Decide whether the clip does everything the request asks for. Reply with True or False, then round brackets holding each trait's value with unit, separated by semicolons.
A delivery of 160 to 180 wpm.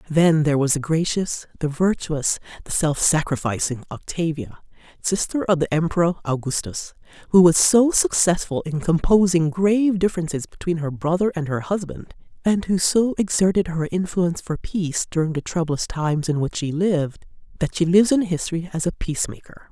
True (165 wpm)